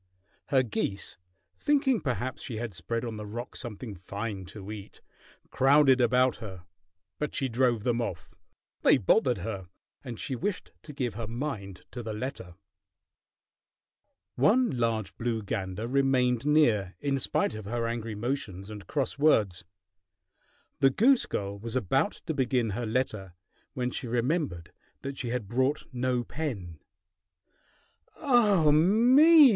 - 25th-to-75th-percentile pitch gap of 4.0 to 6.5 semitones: Yes, average, 4.5 semitones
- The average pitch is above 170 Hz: No, low, 120 Hz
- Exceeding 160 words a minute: No, average, 140 wpm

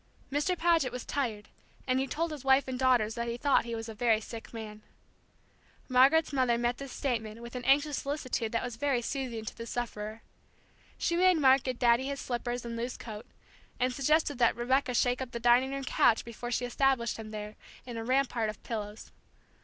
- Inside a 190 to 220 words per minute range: Yes, average, 200 wpm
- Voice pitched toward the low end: No, high, 245 Hz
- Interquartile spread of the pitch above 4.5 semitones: No, average, 2.7 semitones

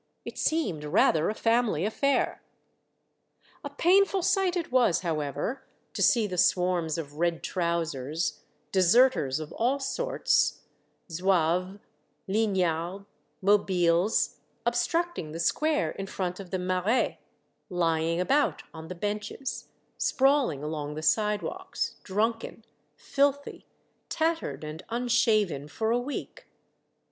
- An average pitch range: No, wide, 7.0 semitones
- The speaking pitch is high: Yes, high, 195 Hz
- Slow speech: Yes, slow, 115 wpm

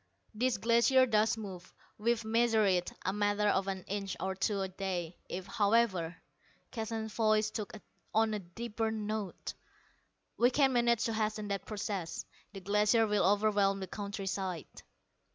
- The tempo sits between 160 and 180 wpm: No, average, 150 wpm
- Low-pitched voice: No, high, 210 Hz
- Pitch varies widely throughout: No, narrow, 2.4 semitones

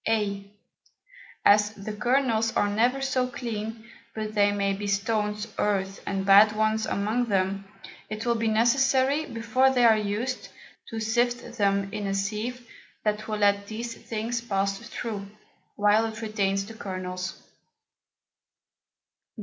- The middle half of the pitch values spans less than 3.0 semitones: Yes, narrow, 2.5 semitones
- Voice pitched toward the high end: Yes, high, 215 Hz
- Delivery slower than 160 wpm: Yes, average, 140 wpm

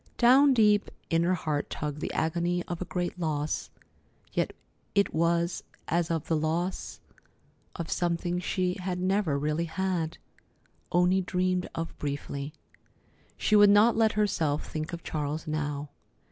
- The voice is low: No, medium, 170 Hz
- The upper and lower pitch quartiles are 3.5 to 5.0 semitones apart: No, average, 2.9 semitones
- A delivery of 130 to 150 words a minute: Yes, average, 140 wpm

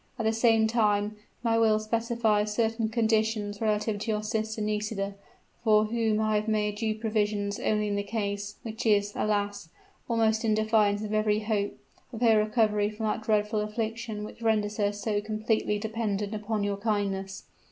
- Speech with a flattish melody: Yes, narrow, 1.1 semitones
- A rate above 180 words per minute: No, average, 170 wpm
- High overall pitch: Yes, high, 215 Hz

